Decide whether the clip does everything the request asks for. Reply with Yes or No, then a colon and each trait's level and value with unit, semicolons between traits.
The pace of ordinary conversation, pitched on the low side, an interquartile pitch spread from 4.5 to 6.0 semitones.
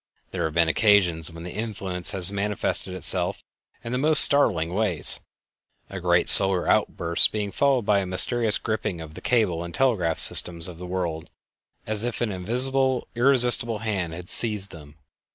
Yes: average, 170 wpm; low, 100 Hz; average, 5.0 semitones